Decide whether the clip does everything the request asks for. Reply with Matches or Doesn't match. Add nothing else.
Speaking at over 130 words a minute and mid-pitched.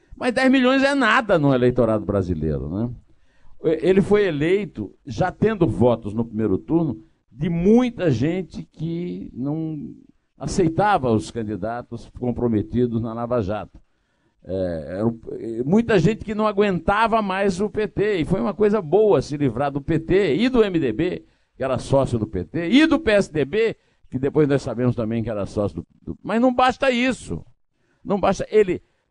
Matches